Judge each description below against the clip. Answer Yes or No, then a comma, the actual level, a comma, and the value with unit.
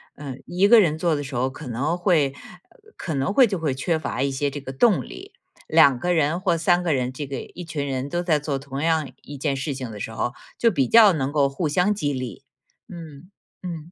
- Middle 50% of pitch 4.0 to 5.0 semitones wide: Yes, average, 4.3 semitones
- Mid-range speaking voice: Yes, medium, 150 Hz